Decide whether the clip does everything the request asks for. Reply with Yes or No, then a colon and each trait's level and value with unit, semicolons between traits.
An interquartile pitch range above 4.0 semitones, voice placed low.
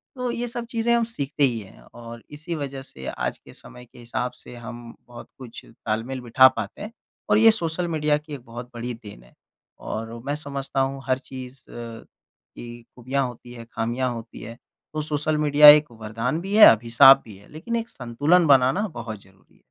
Yes: average, 4.5 semitones; low, 130 Hz